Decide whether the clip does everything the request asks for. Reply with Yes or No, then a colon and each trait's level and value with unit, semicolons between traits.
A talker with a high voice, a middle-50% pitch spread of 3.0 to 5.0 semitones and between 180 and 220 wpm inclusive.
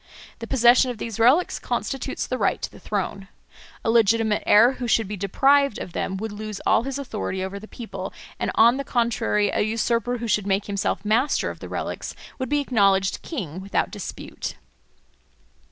Yes: high, 225 Hz; average, 3.5 semitones; average, 185 wpm